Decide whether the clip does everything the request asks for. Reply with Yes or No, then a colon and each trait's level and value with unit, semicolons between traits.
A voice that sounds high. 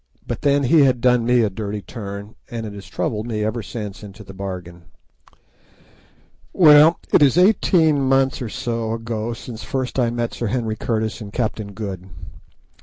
No: low, 115 Hz